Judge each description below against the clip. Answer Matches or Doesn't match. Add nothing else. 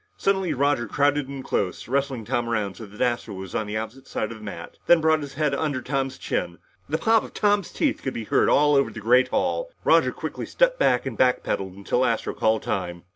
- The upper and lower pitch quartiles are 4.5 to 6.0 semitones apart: Matches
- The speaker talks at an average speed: Doesn't match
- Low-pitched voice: Matches